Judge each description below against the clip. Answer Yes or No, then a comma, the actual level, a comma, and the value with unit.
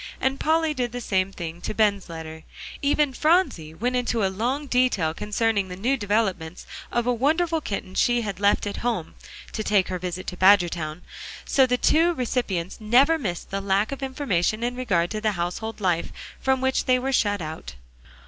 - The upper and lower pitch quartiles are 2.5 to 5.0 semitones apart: No, wide, 5.6 semitones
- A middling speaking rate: Yes, average, 185 wpm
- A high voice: Yes, high, 215 Hz